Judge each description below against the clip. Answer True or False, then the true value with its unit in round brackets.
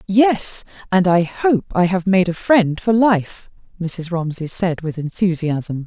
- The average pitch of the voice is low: False (185 Hz)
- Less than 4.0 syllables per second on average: True (3.7 syllables/s)